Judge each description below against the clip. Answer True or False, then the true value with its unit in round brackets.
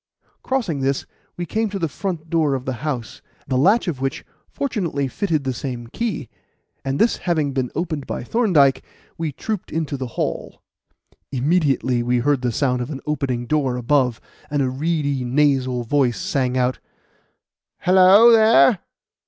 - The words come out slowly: False (160 wpm)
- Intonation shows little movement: False (4.8 semitones)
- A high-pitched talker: False (140 Hz)